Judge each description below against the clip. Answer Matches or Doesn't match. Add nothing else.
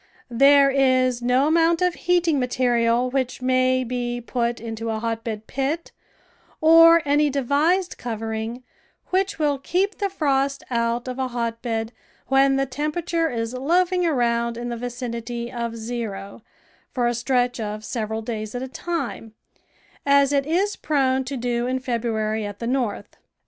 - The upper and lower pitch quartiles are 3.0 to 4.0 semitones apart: Matches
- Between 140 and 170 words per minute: Matches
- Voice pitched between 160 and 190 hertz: Doesn't match